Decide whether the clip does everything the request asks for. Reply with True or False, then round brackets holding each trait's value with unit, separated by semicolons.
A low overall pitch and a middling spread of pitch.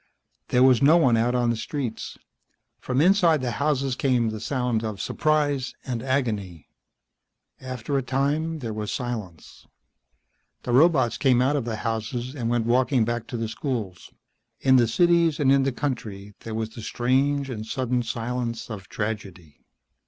True (125 Hz; 3.4 semitones)